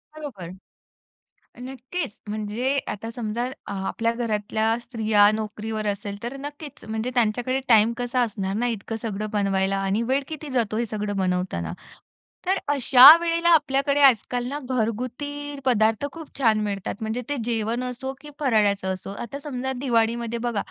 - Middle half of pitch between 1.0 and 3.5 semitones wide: No, average, 3.9 semitones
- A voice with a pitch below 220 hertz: No, high, 235 Hz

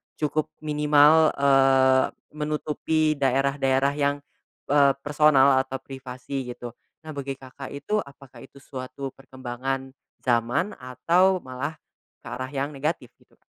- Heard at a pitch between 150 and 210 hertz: No, low, 135 Hz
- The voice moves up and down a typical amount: No, narrow, 2.1 semitones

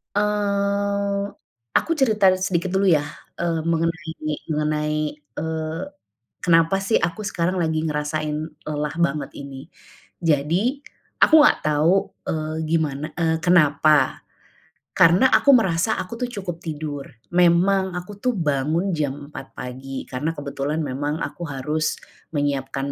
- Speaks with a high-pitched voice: No, medium, 160 Hz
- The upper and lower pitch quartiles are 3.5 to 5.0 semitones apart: Yes, average, 3.8 semitones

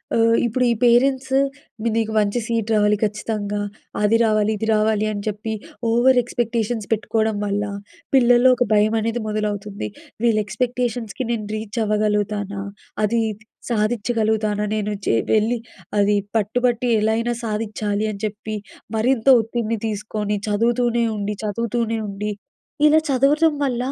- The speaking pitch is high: Yes, high, 220 Hz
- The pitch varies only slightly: Yes, narrow, 2.2 semitones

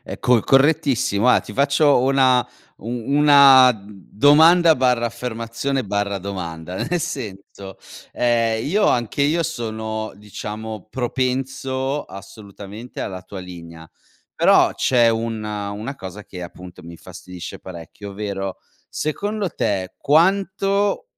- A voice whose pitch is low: Yes, low, 115 Hz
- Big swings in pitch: Yes, wide, 5.7 semitones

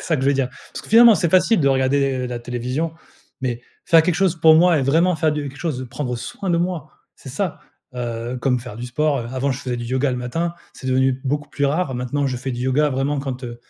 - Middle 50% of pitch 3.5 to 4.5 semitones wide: Yes, average, 4.1 semitones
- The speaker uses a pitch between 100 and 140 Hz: Yes, low, 135 Hz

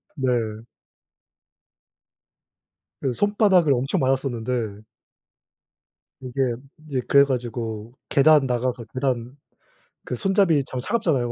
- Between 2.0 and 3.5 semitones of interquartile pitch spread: Yes, average, 3.1 semitones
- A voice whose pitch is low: Yes, low, 130 Hz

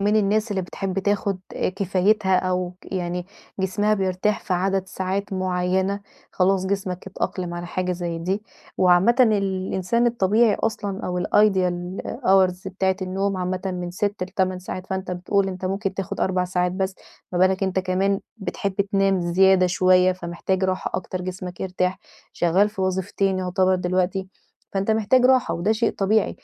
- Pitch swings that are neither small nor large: No, narrow, 1.3 semitones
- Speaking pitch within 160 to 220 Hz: Yes, high, 190 Hz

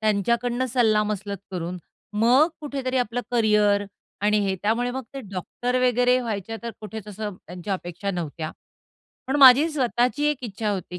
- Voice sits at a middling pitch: No, high, 220 Hz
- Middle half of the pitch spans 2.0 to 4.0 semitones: Yes, average, 3.7 semitones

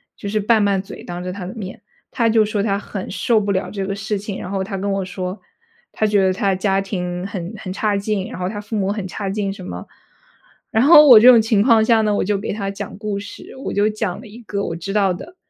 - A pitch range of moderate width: No, narrow, 2.0 semitones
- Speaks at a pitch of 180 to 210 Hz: Yes, high, 200 Hz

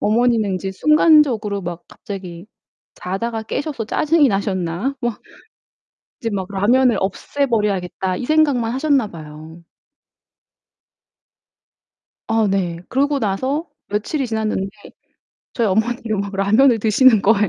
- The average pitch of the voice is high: Yes, high, 215 Hz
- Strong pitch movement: No, average, 5.0 semitones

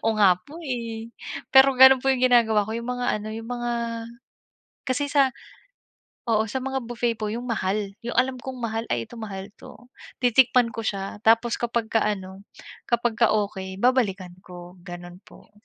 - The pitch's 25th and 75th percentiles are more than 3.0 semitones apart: Yes, average, 3.4 semitones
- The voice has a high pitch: Yes, high, 230 Hz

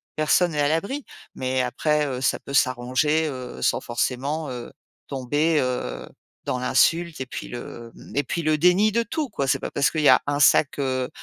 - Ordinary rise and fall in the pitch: Yes, average, 3.7 semitones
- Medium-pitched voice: Yes, medium, 145 Hz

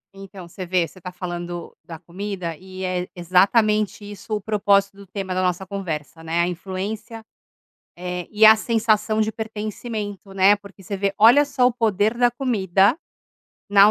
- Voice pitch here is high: Yes, high, 200 Hz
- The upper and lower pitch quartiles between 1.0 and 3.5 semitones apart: Yes, average, 2.9 semitones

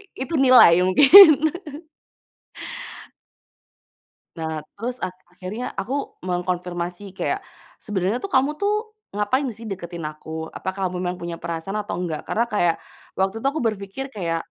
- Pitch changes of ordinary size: No, wide, 6.0 semitones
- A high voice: Yes, high, 195 Hz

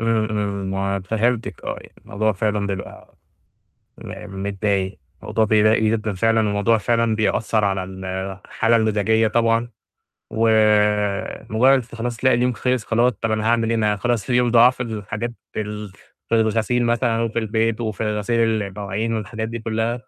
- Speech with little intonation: Yes, narrow, 1.8 semitones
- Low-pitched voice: Yes, low, 110 Hz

